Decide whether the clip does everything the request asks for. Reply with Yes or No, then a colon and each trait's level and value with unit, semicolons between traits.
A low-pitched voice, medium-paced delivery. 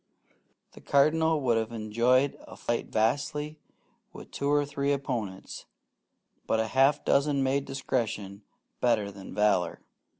No: low, 130 Hz; slow, 130 wpm